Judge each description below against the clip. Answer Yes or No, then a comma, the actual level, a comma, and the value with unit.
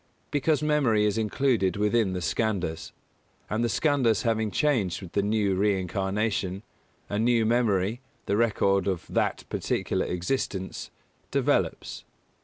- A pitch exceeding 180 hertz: No, low, 105 Hz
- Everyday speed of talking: No, slow, 130 wpm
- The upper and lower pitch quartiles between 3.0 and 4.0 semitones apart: Yes, average, 3.4 semitones